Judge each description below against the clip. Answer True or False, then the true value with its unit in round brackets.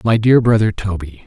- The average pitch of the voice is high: False (105 Hz)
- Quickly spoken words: False (190 wpm)